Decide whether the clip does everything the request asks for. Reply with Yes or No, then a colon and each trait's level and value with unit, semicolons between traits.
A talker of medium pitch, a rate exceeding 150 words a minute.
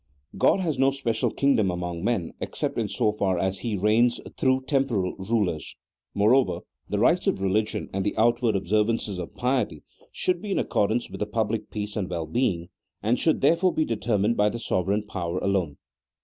No: low, 105 Hz; average, 185 wpm